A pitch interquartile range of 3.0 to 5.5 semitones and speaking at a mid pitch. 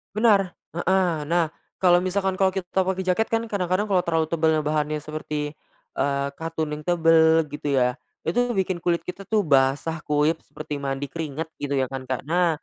Yes: average, 3.6 semitones; medium, 165 Hz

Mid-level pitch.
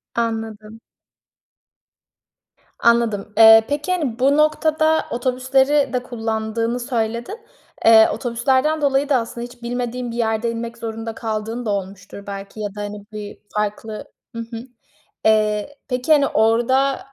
No: high, 230 Hz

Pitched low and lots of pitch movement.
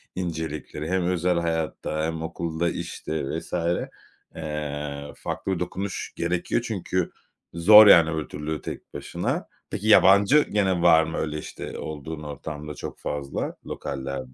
No: very low, 80 Hz; average, 2.9 semitones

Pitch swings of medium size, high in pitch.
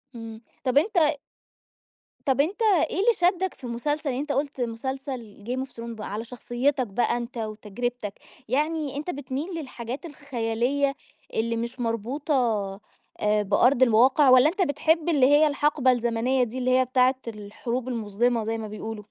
Yes: average, 3.8 semitones; very high, 255 Hz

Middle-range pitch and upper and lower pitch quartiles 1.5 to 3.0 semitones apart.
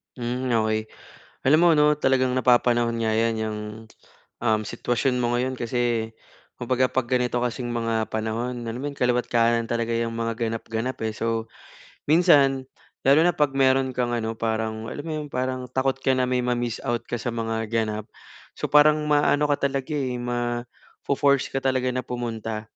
No: low, 120 Hz; narrow, 2.4 semitones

